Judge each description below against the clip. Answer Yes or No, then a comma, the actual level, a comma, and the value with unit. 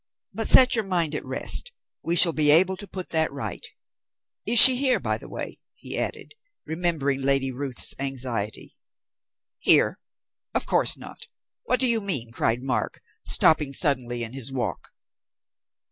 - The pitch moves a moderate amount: No, wide, 6.3 semitones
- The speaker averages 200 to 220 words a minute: No, average, 155 wpm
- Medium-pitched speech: Yes, medium, 150 Hz